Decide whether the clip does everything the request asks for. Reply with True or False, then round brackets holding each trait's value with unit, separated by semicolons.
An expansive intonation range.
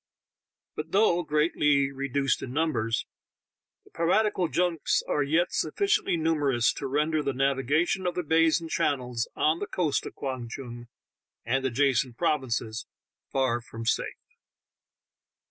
False (4.0 semitones)